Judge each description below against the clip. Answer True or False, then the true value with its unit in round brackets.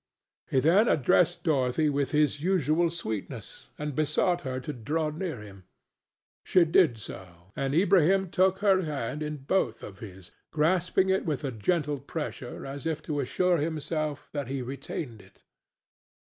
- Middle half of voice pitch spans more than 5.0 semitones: False (4.6 semitones)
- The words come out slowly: False (155 wpm)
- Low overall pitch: False (150 Hz)